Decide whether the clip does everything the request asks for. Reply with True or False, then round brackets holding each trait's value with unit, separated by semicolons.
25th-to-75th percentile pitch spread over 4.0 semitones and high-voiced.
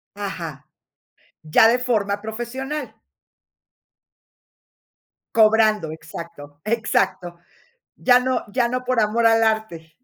True (5.6 semitones; 220 Hz)